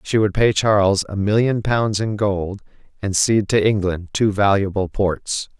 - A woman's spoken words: No, male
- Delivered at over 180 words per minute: No, average, 170 wpm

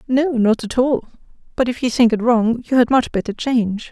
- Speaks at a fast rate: Yes, fast, 230 wpm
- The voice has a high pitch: Yes, high, 240 Hz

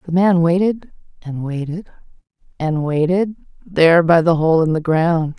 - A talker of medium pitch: Yes, medium, 165 Hz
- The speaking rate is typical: Yes, average, 155 wpm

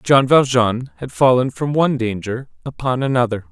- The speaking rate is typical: Yes, average, 155 wpm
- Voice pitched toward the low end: Yes, low, 130 Hz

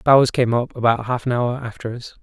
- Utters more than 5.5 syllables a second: Yes, 5.9 syllables/s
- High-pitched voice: No, low, 120 Hz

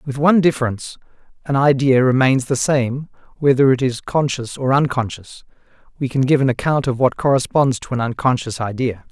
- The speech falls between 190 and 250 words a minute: No, average, 170 wpm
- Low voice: Yes, low, 130 Hz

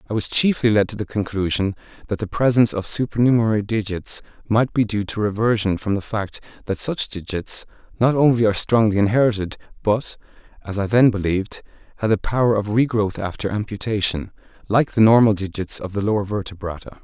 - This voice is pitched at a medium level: No, low, 105 Hz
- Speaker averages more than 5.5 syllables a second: Yes, 5.9 syllables/s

